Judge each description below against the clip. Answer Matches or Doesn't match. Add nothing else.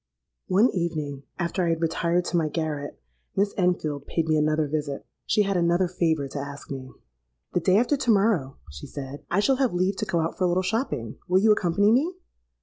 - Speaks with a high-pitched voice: Doesn't match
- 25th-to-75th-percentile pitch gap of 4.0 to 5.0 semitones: Matches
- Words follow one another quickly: Matches